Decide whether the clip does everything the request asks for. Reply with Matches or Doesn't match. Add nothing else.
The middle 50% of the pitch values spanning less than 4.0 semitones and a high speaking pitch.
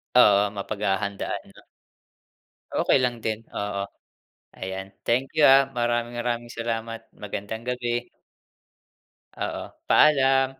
Doesn't match